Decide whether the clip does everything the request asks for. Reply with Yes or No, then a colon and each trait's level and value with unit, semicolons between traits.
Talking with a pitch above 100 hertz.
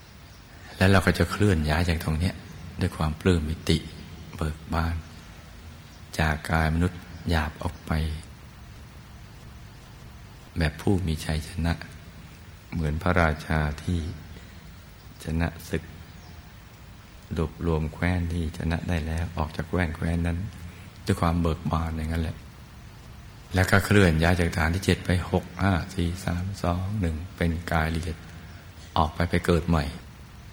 No: very low, 85 Hz